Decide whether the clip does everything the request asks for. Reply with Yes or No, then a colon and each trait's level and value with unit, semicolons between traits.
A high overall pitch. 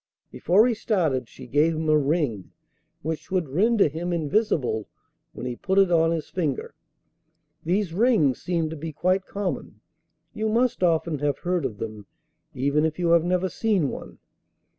No: medium, 165 Hz